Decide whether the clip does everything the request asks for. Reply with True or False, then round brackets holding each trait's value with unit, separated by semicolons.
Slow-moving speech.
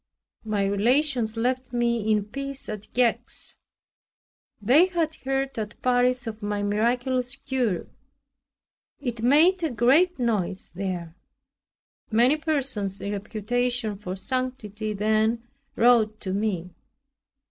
True (115 wpm)